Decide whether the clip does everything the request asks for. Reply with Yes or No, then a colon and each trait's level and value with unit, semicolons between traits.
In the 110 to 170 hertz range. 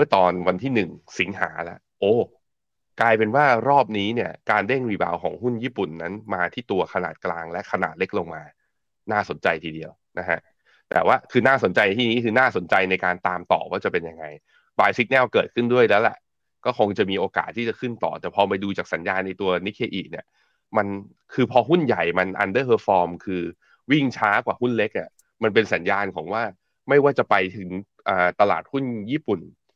No: low, 100 Hz